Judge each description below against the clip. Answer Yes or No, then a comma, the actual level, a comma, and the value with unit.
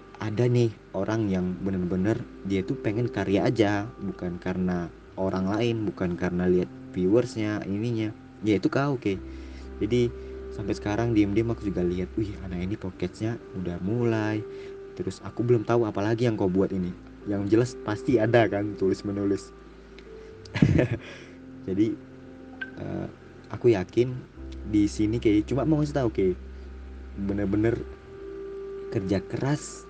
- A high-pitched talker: No, low, 105 Hz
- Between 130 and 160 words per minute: Yes, fast, 140 wpm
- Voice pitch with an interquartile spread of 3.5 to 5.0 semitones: Yes, average, 4.4 semitones